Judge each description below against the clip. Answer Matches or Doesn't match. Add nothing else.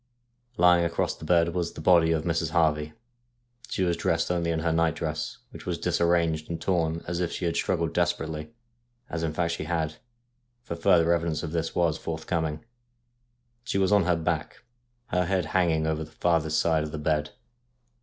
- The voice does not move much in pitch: Matches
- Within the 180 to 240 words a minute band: Matches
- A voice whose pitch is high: Doesn't match